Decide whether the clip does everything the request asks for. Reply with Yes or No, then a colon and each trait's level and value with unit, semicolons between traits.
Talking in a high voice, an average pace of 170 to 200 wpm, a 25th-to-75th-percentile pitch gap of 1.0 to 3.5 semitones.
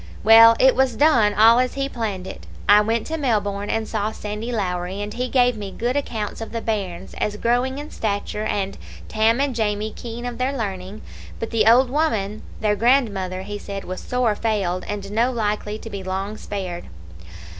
Yes: high, 215 Hz; average, 190 wpm; average, 3.0 semitones